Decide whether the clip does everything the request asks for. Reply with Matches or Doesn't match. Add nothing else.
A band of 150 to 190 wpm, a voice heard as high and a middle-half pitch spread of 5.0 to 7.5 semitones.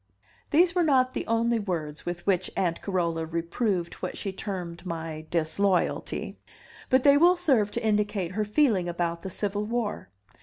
Matches